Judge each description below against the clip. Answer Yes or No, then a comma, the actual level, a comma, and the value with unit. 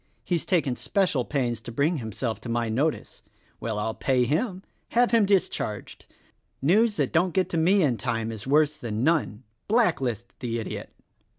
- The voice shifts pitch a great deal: Yes, wide, 7.4 semitones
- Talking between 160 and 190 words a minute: Yes, average, 175 wpm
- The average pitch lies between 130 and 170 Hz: Yes, medium, 140 Hz